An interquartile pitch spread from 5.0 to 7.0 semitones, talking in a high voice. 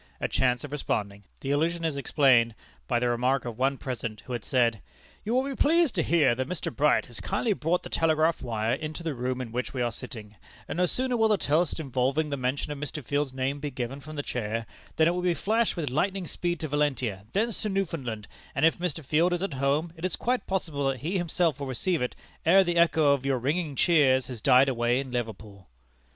No: average, 5.3 semitones; medium, 145 Hz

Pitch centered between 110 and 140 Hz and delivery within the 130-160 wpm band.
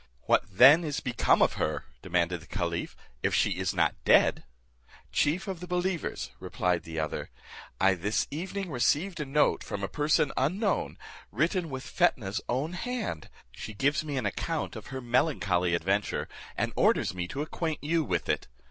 No: low, 135 Hz; average, 170 wpm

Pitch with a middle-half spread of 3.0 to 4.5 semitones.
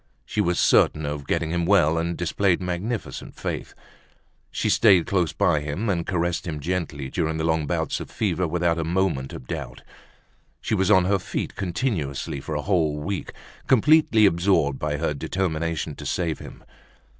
Yes: average, 3.4 semitones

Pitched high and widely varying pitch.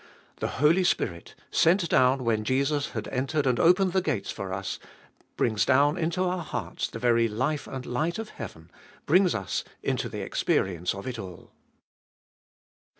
No: low, 130 Hz; wide, 7.1 semitones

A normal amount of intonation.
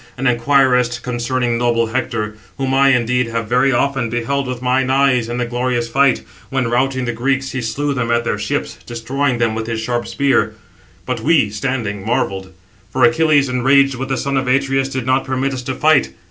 No: narrow, 2.3 semitones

